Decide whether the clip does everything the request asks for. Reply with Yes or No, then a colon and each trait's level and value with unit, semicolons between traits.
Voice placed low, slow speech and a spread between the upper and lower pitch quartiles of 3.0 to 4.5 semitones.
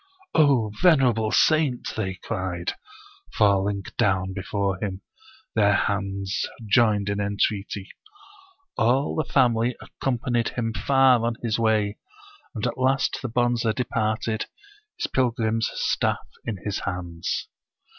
Yes: low, 110 Hz; slow, 120 wpm; average, 3.5 semitones